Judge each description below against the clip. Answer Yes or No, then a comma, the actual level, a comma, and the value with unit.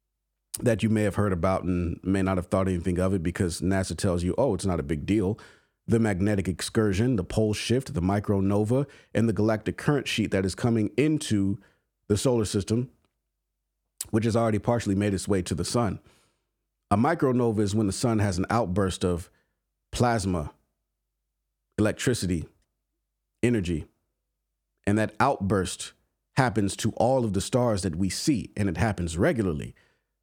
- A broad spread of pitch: No, average, 3.7 semitones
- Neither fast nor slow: Yes, average, 165 wpm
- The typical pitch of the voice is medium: No, low, 100 Hz